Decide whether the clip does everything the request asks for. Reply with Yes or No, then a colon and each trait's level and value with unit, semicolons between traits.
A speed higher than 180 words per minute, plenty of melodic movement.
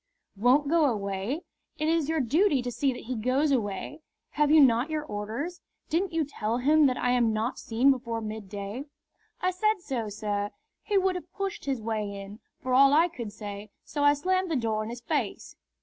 Yes: average, 200 wpm; wide, 6.0 semitones